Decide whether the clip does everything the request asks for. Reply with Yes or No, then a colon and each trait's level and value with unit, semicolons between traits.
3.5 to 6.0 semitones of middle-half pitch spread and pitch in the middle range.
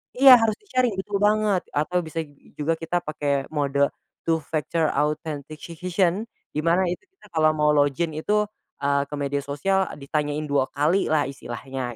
Yes: average, 3.9 semitones; medium, 155 Hz